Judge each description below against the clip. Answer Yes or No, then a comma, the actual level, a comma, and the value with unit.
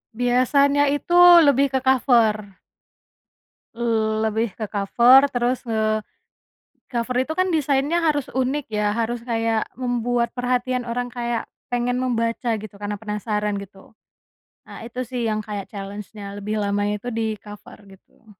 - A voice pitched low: No, high, 230 Hz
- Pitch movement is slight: No, average, 3.1 semitones